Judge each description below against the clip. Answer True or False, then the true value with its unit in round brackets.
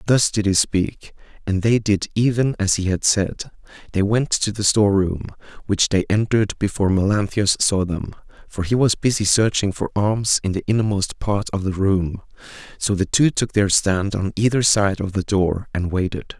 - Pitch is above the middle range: False (100 Hz)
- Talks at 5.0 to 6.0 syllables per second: False (4.8 syllables/s)